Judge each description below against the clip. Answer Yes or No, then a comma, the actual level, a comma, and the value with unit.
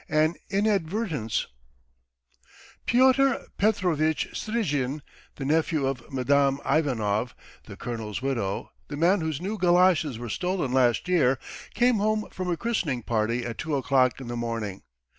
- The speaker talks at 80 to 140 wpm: Yes, slow, 135 wpm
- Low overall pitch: No, medium, 145 Hz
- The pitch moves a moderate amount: No, wide, 6.8 semitones